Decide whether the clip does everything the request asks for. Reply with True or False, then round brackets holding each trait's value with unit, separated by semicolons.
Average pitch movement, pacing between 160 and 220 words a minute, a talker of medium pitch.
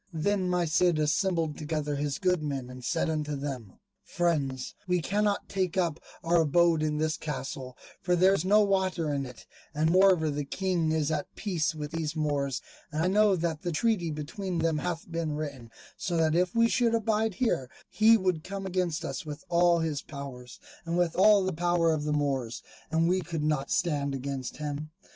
True (3.6 semitones; 195 wpm; 160 Hz)